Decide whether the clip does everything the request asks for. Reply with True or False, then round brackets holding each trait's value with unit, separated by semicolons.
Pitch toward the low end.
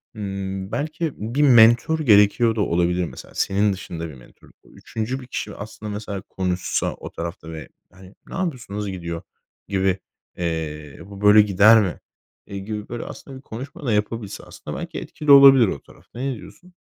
True (105 Hz)